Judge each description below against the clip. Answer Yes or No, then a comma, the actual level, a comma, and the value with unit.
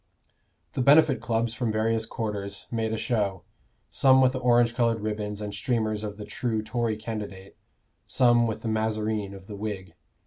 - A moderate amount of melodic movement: No, narrow, 2.0 semitones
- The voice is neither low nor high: No, low, 110 Hz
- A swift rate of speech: No, average, 170 wpm